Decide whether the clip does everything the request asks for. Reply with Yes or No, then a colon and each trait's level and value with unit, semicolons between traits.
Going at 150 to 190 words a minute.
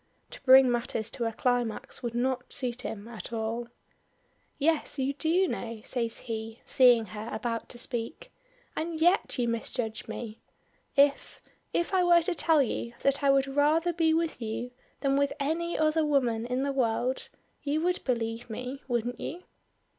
Yes: average, 170 wpm